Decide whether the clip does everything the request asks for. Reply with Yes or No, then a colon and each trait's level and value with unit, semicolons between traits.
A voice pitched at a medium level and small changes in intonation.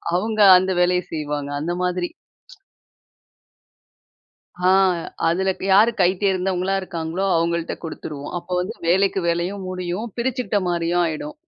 Yes: medium, 180 Hz; narrow, 2.2 semitones